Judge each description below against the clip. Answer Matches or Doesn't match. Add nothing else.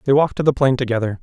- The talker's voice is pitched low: Matches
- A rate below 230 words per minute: Doesn't match